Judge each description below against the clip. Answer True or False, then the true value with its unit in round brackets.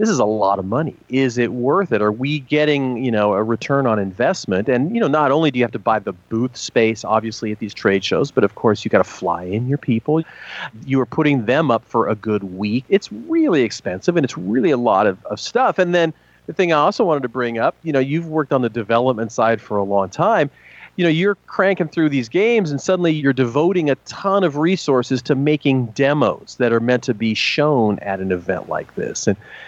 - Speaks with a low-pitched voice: True (130 Hz)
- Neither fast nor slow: False (240 wpm)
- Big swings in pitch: True (5.8 semitones)